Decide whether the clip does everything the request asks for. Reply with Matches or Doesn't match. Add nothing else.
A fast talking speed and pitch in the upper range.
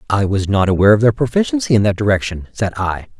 Doesn't match